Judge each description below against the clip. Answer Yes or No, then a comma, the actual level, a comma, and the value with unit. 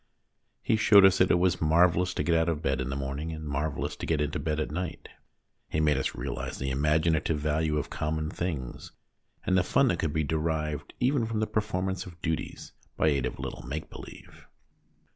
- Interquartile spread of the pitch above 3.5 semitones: No, average, 3.2 semitones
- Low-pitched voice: Yes, very low, 80 Hz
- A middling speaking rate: No, fast, 210 wpm